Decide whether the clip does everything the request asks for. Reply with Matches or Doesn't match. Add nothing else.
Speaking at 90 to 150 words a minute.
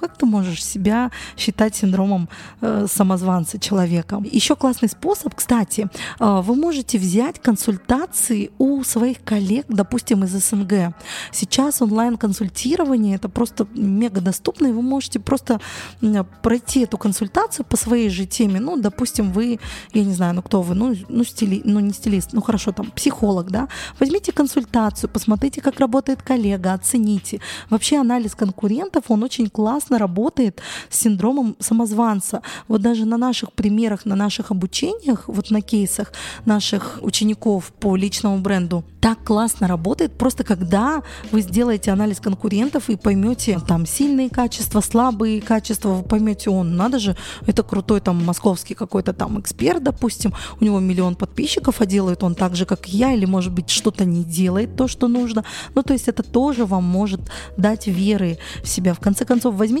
Doesn't match